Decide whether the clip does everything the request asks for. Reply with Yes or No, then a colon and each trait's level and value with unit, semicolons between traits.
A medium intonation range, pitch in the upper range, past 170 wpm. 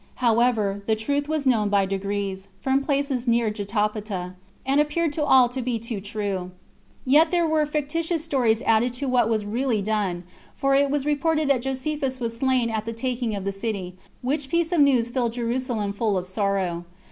Yes: average, 5.0 semitones; high, 240 Hz; average, 190 wpm